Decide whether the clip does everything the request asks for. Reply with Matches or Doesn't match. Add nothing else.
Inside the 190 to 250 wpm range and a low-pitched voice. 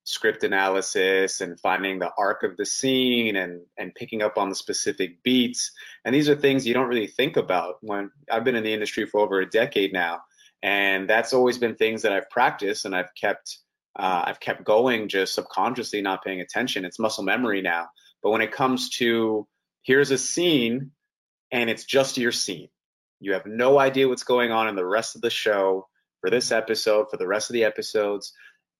Matches